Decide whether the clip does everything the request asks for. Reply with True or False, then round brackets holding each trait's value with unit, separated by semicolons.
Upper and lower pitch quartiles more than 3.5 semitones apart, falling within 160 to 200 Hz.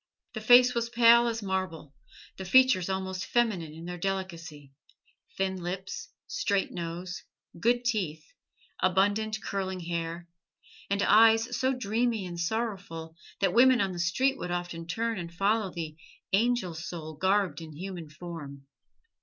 True (4.8 semitones; 190 Hz)